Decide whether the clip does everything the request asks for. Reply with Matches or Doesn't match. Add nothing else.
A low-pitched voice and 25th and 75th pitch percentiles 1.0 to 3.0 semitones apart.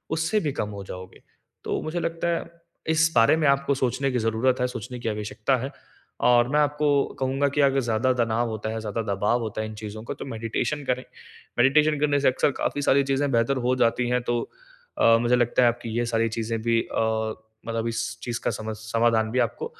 Doesn't match